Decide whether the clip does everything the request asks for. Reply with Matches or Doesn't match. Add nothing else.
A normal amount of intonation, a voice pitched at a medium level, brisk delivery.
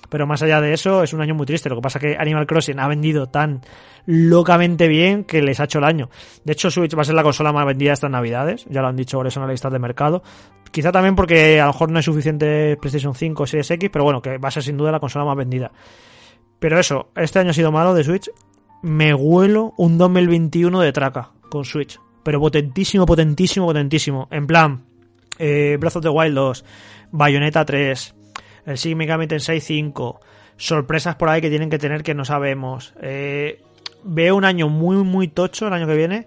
Matches